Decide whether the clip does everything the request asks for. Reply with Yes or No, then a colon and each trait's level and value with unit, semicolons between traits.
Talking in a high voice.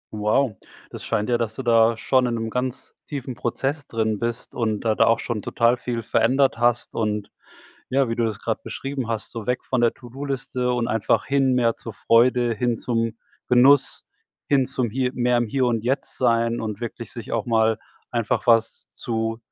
No: low, 120 Hz